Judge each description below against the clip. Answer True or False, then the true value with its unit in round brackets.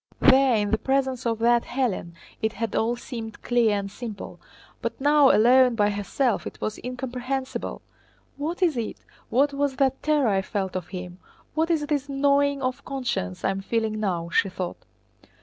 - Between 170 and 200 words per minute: True (175 wpm)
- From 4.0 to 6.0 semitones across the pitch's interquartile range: True (4.7 semitones)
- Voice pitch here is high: True (245 Hz)